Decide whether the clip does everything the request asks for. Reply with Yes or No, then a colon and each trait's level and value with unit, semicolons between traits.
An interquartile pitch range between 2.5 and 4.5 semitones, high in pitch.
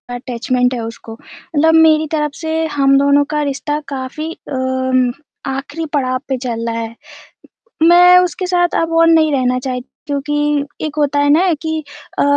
Yes: average, 3.5 semitones; very high, 285 Hz